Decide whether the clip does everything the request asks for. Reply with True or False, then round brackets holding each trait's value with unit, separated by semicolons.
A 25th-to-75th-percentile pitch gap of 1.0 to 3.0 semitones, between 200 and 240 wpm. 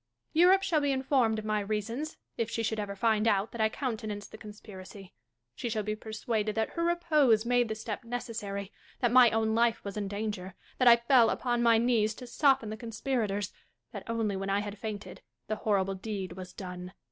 True (2.6 semitones; 205 wpm)